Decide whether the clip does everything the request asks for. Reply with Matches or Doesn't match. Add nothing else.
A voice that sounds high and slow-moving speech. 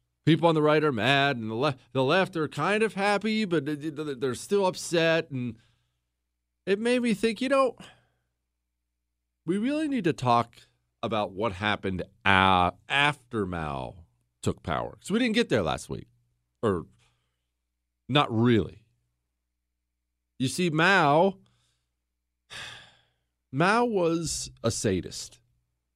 Doesn't match